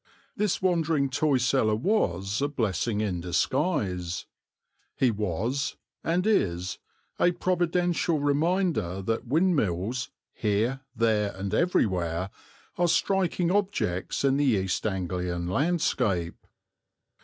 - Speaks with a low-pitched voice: Yes, low, 120 Hz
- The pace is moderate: No, slow, 105 wpm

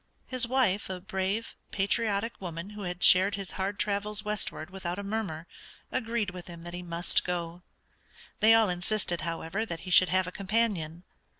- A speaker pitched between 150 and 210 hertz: Yes, high, 190 Hz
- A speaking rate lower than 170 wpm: No, average, 175 wpm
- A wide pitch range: No, average, 3.2 semitones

